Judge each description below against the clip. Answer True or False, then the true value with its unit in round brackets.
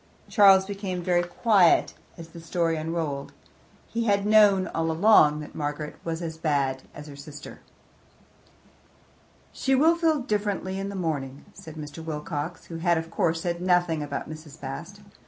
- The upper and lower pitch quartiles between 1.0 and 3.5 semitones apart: False (4.2 semitones)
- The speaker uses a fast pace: False (155 wpm)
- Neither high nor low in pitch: True (165 Hz)